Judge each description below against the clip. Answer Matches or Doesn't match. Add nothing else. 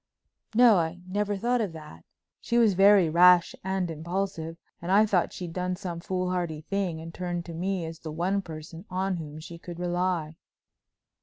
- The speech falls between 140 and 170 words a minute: Doesn't match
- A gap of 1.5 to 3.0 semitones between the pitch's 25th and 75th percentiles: Matches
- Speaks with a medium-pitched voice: Matches